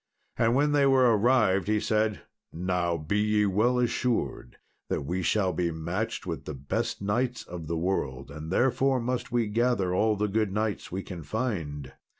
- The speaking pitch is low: Yes, low, 105 Hz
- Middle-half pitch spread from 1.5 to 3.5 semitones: No, average, 5.1 semitones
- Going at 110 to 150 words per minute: No, average, 175 wpm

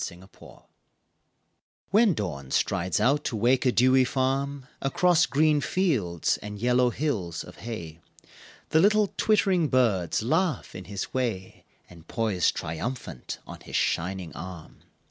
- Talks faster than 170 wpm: No, slow, 135 wpm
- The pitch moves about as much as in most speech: No, wide, 7.7 semitones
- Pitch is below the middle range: Yes, low, 120 Hz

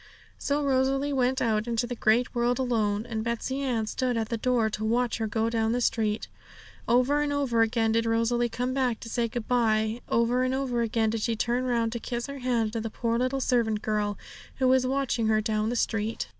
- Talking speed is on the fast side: Yes, fast, 220 wpm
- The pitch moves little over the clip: Yes, narrow, 2.2 semitones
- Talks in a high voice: Yes, high, 235 Hz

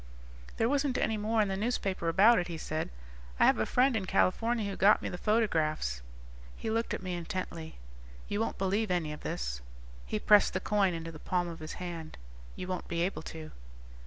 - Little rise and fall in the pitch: No, average, 4.5 semitones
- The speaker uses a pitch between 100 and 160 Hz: No, medium, 185 Hz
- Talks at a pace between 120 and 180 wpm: No, fast, 205 wpm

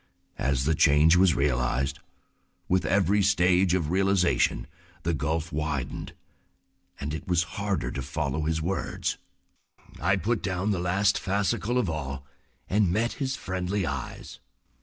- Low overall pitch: Yes, very low, 90 Hz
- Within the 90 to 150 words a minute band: Yes, average, 140 wpm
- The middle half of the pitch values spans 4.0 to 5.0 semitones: Yes, average, 4.7 semitones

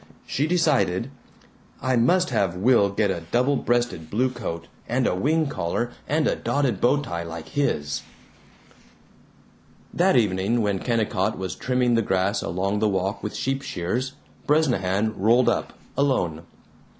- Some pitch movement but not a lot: No, wide, 5.7 semitones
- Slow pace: No, average, 145 wpm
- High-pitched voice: No, low, 115 Hz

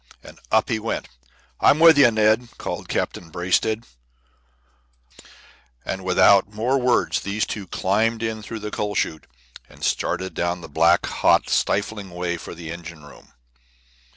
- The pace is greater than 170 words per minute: No, average, 150 wpm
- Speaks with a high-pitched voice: No, low, 100 Hz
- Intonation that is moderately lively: Yes, average, 4.2 semitones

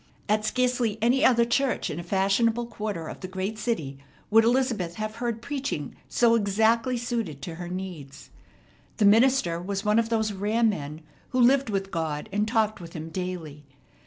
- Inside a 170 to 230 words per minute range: Yes, average, 175 wpm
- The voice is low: No, high, 215 Hz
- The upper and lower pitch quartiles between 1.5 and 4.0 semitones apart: No, average, 4.7 semitones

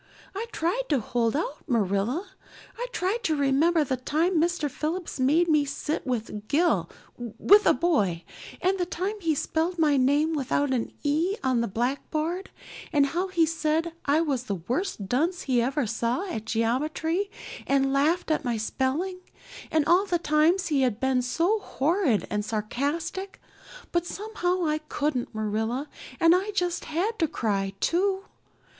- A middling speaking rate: Yes, average, 160 wpm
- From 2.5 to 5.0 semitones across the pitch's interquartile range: No, wide, 5.6 semitones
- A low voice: No, very high, 305 Hz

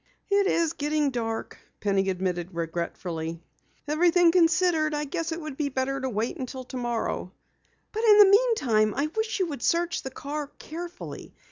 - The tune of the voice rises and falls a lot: Yes, wide, 7.2 semitones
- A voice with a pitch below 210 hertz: No, very high, 290 Hz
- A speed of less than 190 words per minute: Yes, average, 160 wpm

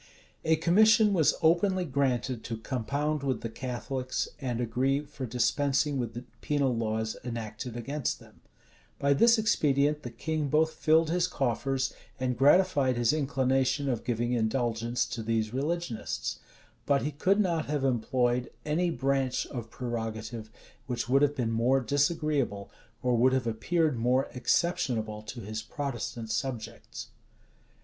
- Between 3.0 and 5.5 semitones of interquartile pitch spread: Yes, average, 4.0 semitones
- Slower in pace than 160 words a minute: Yes, average, 140 wpm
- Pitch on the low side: Yes, low, 130 Hz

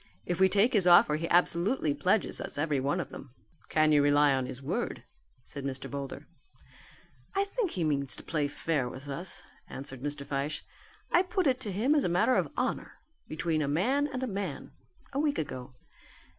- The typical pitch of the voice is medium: Yes, medium, 155 Hz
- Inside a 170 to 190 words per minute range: Yes, average, 185 wpm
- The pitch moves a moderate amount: No, wide, 6.5 semitones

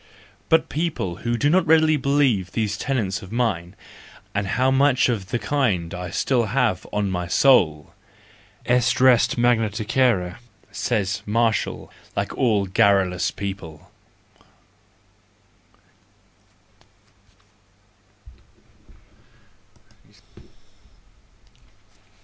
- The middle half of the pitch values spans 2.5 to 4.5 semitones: No, average, 5.3 semitones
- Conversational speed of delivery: No, slow, 85 wpm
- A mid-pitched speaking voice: No, low, 110 Hz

